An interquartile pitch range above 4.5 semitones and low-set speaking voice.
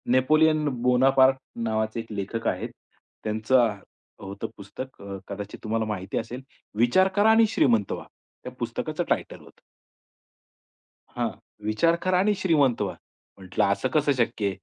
Yes: wide, 5.4 semitones; low, 120 Hz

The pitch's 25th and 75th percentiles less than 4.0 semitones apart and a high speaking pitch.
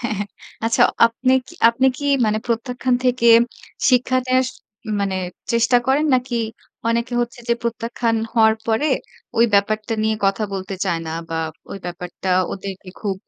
Yes: average, 3.4 semitones; high, 230 Hz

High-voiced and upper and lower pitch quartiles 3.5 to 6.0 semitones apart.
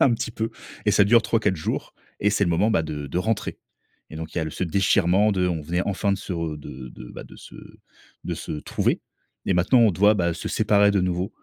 No: very low, 90 Hz; average, 3.8 semitones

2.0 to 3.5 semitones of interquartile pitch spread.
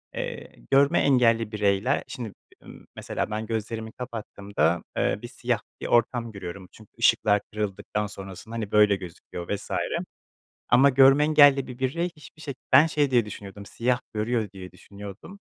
No: average, 4.3 semitones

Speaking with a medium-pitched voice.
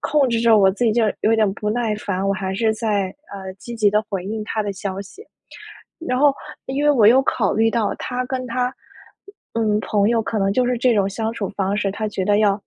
No: high, 215 Hz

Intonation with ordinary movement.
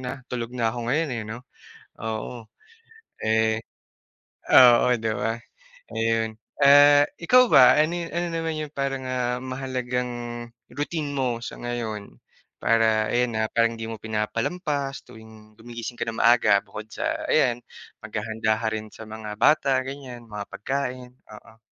Yes: average, 3.4 semitones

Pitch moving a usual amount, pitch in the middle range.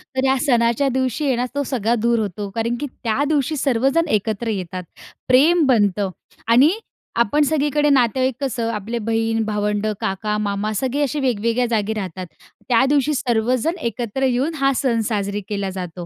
No: average, 4.2 semitones; high, 235 Hz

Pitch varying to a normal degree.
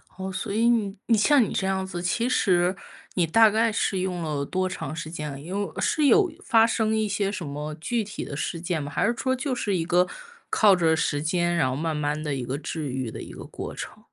No: wide, 5.7 semitones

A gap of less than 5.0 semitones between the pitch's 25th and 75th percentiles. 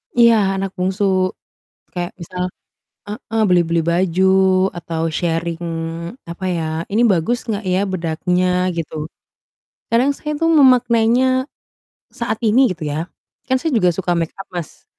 No: wide, 5.5 semitones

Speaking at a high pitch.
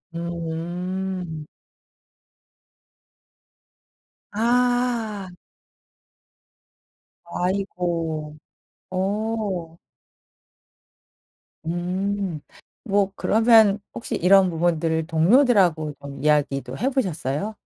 No: medium, 180 Hz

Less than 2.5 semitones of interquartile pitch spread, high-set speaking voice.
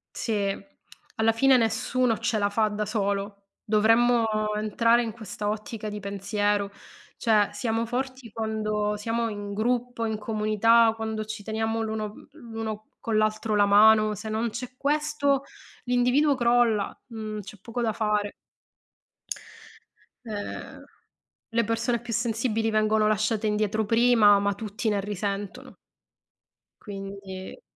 Yes: narrow, 1.8 semitones; high, 220 Hz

